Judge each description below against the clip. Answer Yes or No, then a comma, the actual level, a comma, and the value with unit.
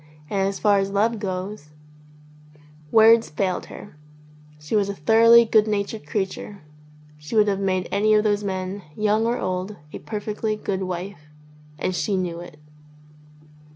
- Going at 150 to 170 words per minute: Yes, average, 155 wpm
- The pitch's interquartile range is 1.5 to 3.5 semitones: Yes, narrow, 2.6 semitones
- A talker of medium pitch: No, high, 200 Hz